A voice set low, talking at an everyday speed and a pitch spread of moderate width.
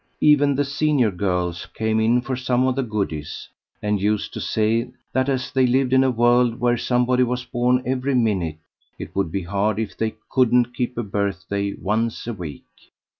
Yes: low, 120 Hz; average, 185 wpm; average, 3.7 semitones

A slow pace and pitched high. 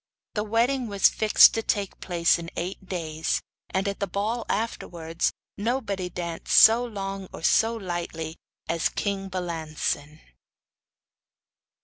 Yes: slow, 125 wpm; high, 195 Hz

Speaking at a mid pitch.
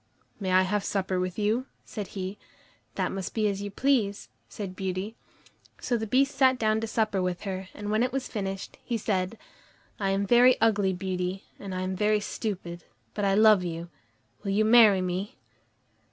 No: high, 200 Hz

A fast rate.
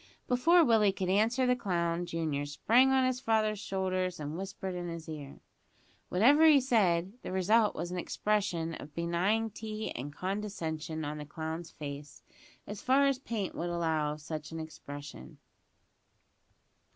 No: average, 150 wpm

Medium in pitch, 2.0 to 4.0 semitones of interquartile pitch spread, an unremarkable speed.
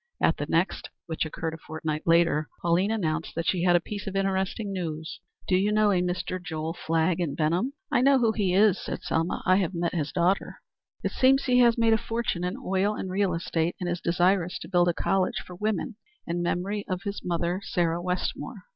No: medium, 180 Hz; average, 2.9 semitones; fast, 215 wpm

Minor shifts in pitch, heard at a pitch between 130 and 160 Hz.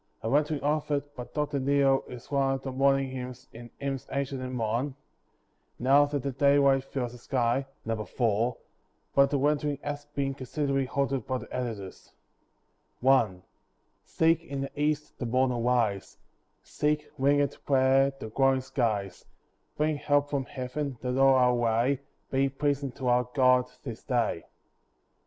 Yes: narrow, 2.3 semitones; low, 135 Hz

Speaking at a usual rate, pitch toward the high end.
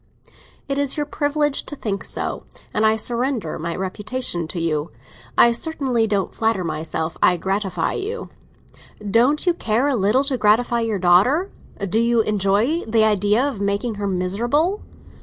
Yes: average, 160 wpm; high, 220 Hz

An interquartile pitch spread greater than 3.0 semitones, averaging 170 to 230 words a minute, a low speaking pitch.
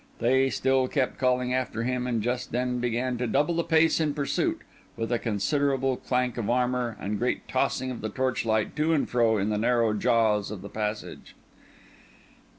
No: narrow, 2.5 semitones; average, 180 wpm; low, 125 Hz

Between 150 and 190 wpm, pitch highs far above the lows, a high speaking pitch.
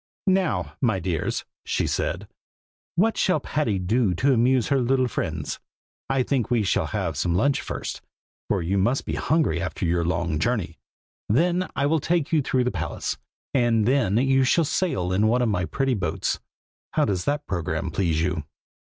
No: average, 175 wpm; wide, 7.0 semitones; low, 115 Hz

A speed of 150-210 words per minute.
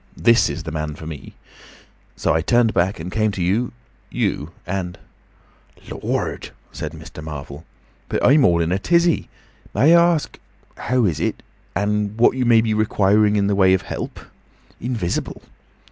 Yes: average, 155 wpm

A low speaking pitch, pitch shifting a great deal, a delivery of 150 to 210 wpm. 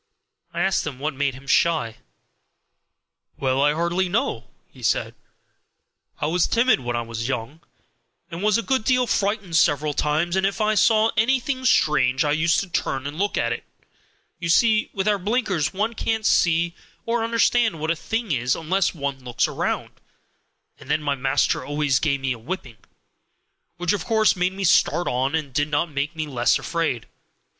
No: medium, 165 Hz; wide, 6.6 semitones; average, 180 wpm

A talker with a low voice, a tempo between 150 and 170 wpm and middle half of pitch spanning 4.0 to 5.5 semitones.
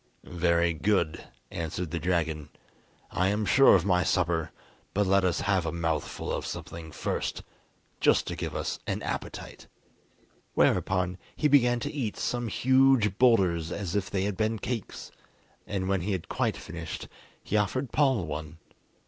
Yes: very low, 95 Hz; average, 155 wpm; average, 4.3 semitones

